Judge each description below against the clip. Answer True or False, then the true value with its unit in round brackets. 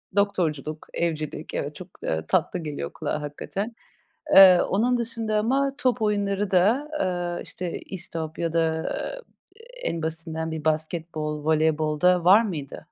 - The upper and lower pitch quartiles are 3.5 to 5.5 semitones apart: True (4.4 semitones)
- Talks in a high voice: False (170 Hz)